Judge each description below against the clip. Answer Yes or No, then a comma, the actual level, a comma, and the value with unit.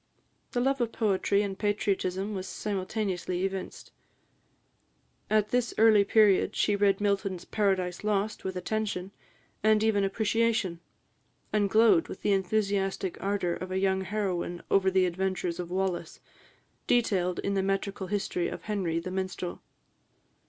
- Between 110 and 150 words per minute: Yes, average, 140 wpm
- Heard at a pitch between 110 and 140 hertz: No, high, 195 Hz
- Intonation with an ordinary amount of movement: No, narrow, 2.2 semitones